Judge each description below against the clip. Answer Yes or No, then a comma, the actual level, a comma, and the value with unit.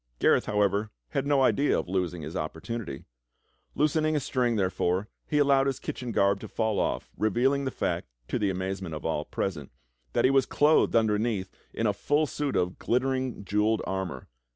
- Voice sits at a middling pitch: No, low, 110 Hz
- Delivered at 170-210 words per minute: Yes, average, 185 wpm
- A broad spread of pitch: Yes, wide, 6.1 semitones